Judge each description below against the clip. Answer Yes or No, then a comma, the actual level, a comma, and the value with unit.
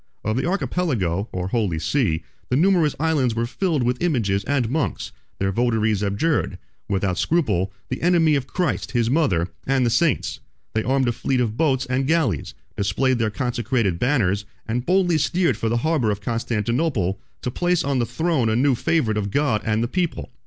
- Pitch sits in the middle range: No, low, 125 Hz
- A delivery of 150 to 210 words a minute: Yes, average, 180 wpm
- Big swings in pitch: Yes, wide, 6.0 semitones